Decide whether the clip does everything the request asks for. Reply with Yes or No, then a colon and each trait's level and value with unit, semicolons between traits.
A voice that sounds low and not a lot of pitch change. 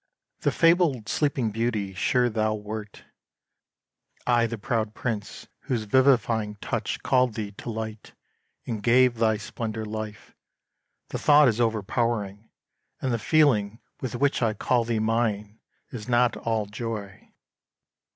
Yes: low, 115 Hz; narrow, 2.3 semitones